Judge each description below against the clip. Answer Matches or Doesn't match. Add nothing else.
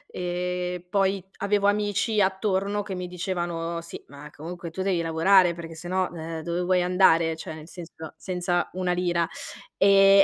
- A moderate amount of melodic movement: Doesn't match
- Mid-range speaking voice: Matches